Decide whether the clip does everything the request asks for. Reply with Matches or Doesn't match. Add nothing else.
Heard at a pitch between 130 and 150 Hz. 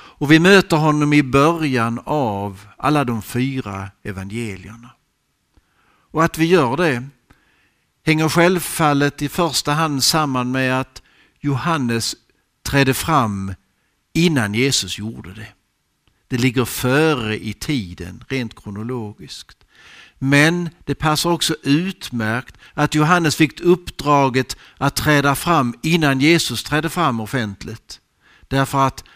Matches